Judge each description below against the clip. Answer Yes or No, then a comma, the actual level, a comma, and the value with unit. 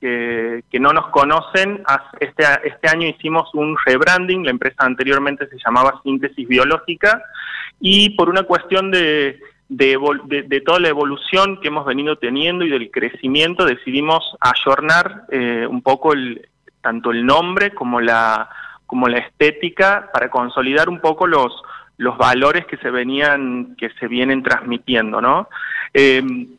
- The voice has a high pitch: No, medium, 140 Hz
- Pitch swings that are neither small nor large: Yes, average, 4.2 semitones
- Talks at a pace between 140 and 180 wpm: Yes, average, 150 wpm